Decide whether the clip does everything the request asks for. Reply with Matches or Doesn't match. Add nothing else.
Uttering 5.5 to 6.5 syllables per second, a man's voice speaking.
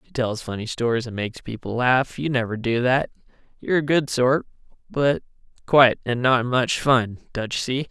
Doesn't match